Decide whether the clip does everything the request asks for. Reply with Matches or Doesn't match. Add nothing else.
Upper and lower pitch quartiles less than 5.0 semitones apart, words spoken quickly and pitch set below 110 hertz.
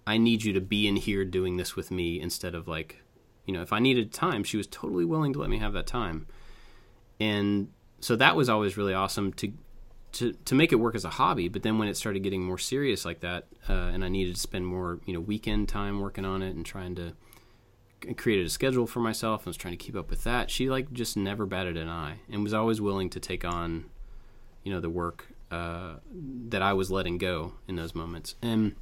Matches